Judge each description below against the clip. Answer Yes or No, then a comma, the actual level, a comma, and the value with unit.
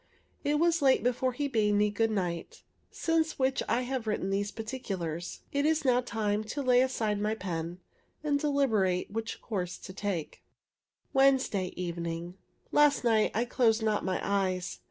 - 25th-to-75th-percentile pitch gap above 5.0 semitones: Yes, wide, 5.5 semitones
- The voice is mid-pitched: No, high, 220 Hz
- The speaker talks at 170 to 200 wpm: No, average, 160 wpm